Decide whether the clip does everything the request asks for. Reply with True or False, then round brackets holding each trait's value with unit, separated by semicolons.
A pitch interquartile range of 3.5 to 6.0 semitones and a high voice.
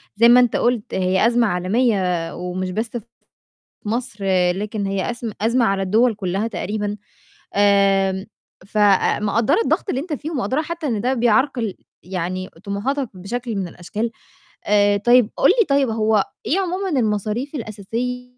True (4.0 semitones; 215 Hz)